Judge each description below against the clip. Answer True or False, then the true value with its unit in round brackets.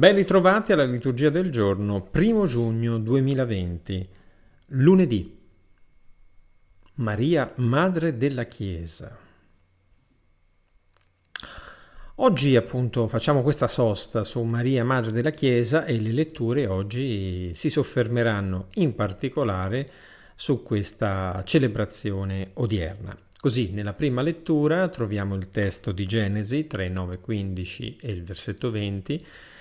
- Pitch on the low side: True (115 Hz)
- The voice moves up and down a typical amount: False (6.2 semitones)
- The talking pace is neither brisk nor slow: False (105 wpm)